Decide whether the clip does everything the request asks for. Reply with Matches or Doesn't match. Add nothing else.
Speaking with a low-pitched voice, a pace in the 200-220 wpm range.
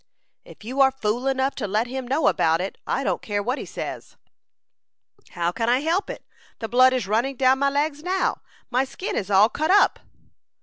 Doesn't match